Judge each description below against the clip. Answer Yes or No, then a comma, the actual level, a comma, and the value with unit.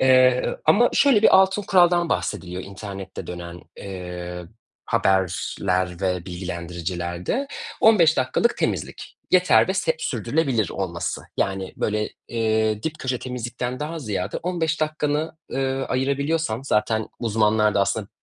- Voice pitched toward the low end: Yes, low, 110 Hz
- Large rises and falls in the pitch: Yes, wide, 8.6 semitones